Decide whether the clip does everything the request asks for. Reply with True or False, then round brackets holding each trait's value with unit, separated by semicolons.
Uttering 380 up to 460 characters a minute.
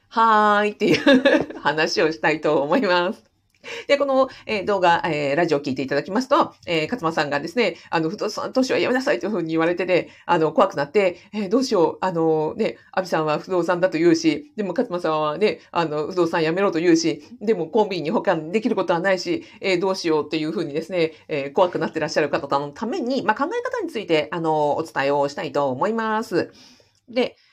True (395 characters per minute)